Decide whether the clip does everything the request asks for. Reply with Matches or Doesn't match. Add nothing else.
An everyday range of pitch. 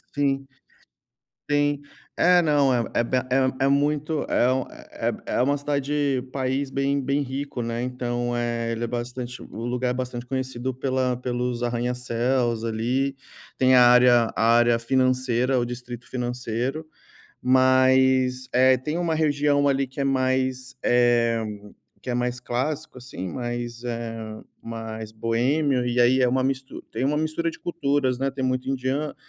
Doesn't match